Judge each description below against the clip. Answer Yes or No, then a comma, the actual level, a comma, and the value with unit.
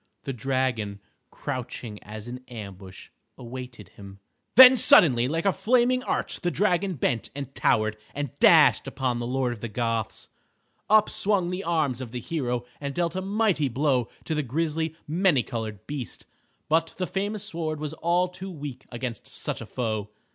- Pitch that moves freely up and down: Yes, wide, 6.6 semitones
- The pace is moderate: Yes, average, 170 wpm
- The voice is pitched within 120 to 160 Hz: Yes, low, 135 Hz